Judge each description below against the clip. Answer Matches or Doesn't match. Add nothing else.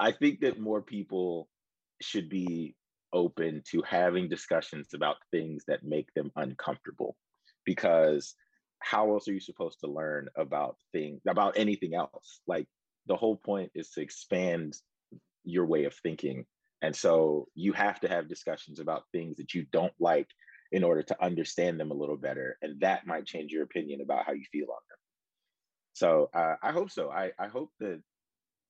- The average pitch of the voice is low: Matches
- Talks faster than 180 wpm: Doesn't match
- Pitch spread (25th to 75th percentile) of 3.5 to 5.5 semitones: Matches